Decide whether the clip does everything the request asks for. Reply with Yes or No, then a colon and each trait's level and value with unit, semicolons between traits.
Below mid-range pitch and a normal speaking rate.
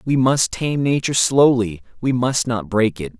Yes: low, 125 Hz; average, 190 wpm